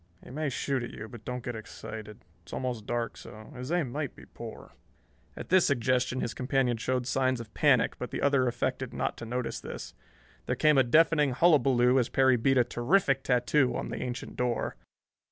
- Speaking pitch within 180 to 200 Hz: No, low, 125 Hz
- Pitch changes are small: Yes, narrow, 2.2 semitones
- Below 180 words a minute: No, average, 195 wpm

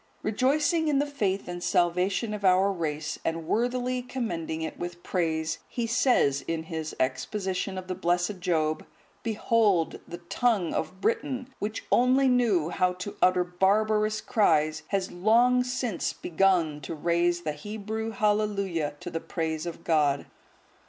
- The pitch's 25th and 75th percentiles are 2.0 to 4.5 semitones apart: No, average, 5.0 semitones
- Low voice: No, medium, 185 Hz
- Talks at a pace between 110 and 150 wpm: Yes, average, 145 wpm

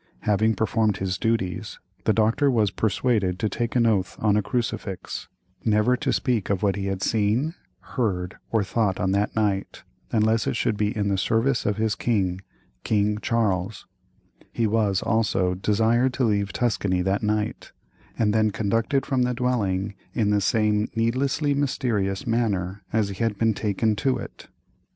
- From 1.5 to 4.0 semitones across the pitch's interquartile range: Yes, narrow, 2.6 semitones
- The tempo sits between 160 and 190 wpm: Yes, average, 165 wpm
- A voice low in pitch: Yes, low, 105 Hz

